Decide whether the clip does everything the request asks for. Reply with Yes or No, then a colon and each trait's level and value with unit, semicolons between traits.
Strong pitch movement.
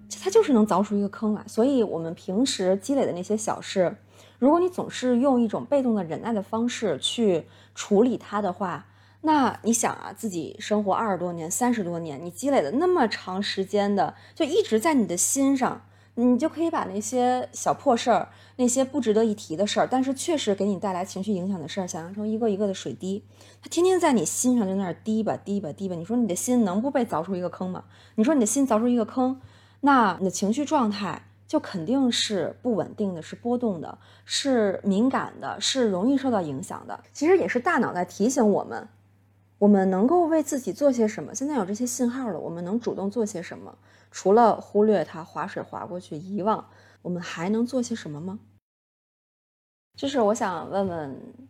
No: average, 4.9 semitones